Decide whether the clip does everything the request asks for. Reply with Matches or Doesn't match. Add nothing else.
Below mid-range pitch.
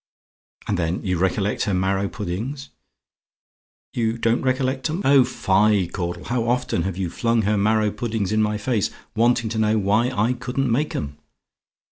Matches